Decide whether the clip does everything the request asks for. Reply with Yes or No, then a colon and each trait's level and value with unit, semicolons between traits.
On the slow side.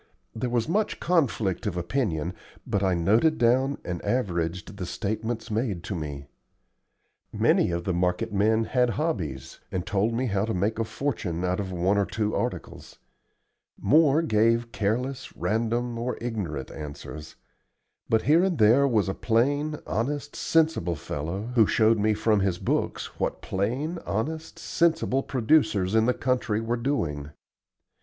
No: average, 150 wpm